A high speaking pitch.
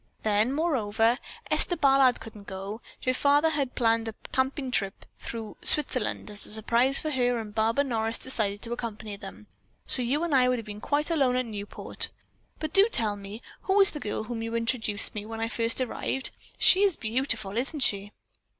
Yes: high, 235 Hz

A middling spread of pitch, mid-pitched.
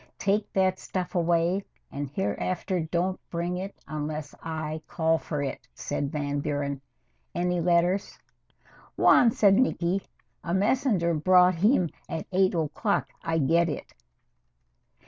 Yes: average, 3.3 semitones; medium, 170 Hz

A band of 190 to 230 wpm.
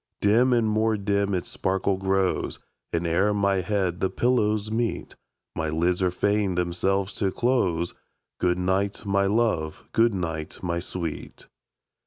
No: average, 145 wpm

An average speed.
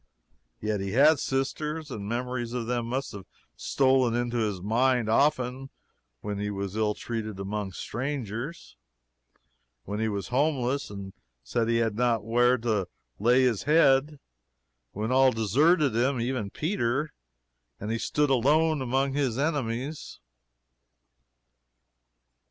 No: slow, 130 wpm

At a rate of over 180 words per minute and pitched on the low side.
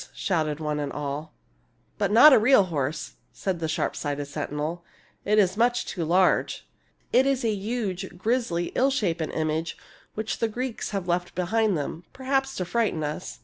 No: average, 190 wpm; medium, 180 Hz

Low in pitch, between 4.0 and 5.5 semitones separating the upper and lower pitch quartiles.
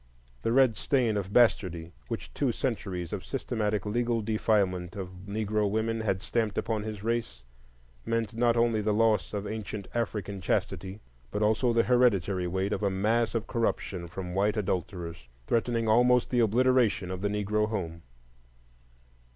No: low, 105 Hz; average, 3.2 semitones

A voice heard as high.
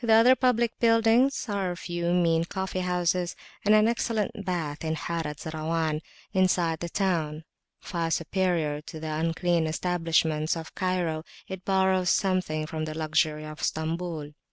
No: medium, 170 Hz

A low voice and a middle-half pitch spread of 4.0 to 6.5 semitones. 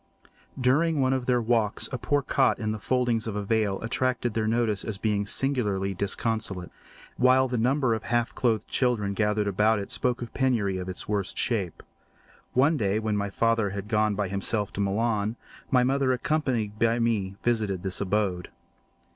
No: low, 110 Hz; average, 3.4 semitones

